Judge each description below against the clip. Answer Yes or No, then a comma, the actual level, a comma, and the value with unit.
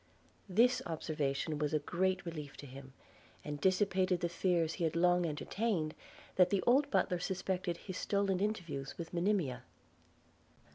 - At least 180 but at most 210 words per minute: No, average, 145 wpm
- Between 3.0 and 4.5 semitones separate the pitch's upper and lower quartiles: Yes, average, 3.6 semitones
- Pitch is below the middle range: No, medium, 175 Hz